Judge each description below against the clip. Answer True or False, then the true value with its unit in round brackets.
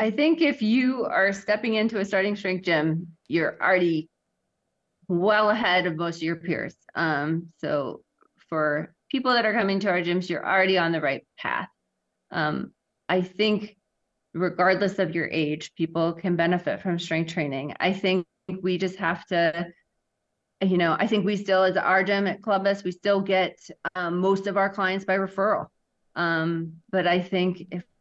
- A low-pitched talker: False (185 Hz)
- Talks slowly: False (175 wpm)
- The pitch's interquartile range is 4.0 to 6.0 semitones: False (2.9 semitones)